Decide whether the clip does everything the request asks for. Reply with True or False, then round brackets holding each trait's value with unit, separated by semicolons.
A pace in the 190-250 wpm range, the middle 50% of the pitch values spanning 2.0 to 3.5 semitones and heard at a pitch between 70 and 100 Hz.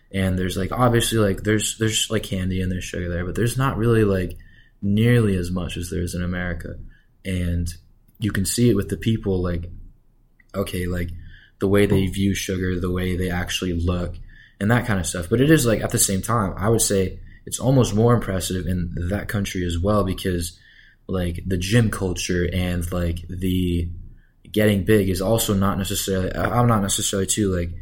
True (195 wpm; 3.1 semitones; 95 Hz)